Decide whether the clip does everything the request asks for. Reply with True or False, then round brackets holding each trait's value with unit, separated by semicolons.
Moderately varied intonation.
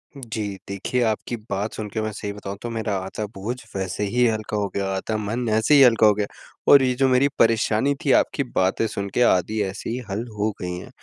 True (3.0 semitones)